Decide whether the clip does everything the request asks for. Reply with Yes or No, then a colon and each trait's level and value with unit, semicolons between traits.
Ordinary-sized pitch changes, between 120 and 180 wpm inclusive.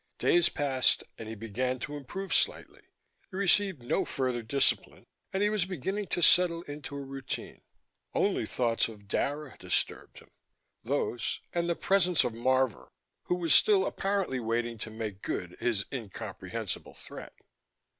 No: wide, 7.3 semitones; average, 150 wpm